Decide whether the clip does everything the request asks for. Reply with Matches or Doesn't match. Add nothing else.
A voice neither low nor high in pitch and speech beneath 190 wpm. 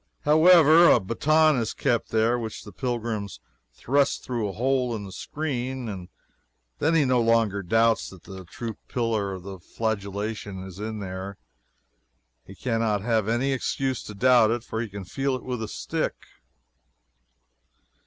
Doesn't match